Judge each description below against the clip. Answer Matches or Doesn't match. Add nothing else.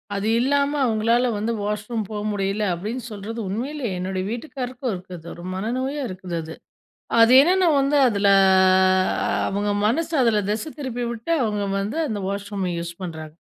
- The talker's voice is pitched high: Matches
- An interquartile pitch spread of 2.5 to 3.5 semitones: Doesn't match